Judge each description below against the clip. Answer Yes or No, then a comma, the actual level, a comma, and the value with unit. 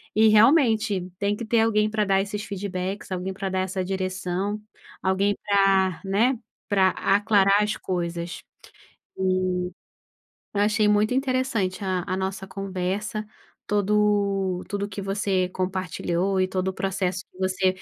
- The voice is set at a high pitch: Yes, high, 195 Hz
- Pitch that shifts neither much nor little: No, narrow, 1.9 semitones